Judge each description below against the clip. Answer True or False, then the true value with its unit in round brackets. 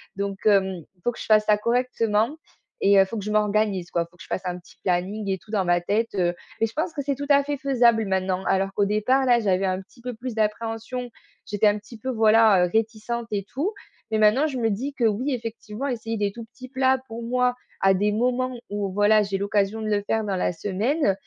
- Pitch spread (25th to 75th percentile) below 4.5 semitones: True (3.5 semitones)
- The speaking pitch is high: True (215 Hz)